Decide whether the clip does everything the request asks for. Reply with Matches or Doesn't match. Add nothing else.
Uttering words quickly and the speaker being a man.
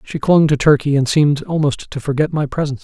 Matches